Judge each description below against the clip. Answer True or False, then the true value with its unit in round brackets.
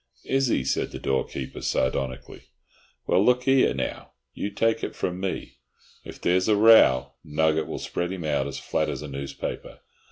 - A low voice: True (80 Hz)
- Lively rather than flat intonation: True (7.3 semitones)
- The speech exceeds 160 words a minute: True (170 wpm)